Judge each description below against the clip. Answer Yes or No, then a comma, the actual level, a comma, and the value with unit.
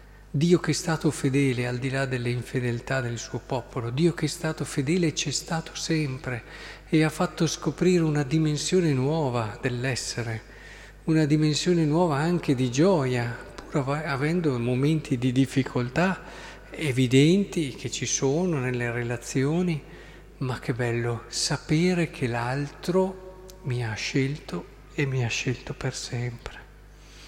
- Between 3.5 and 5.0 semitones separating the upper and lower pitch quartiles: Yes, average, 4.2 semitones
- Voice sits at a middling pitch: Yes, medium, 145 Hz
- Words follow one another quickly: No, average, 135 wpm